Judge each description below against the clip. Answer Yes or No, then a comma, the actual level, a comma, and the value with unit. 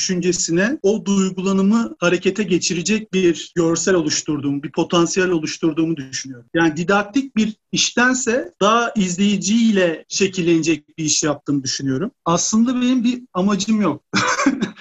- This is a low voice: No, medium, 185 Hz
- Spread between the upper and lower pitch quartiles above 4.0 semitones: Yes, average, 4.4 semitones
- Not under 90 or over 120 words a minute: Yes, average, 115 wpm